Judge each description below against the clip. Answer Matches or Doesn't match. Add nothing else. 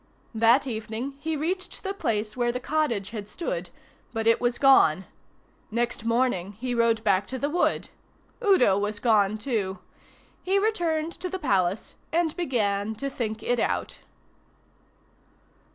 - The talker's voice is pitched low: Doesn't match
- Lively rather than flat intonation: Matches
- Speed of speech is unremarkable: Matches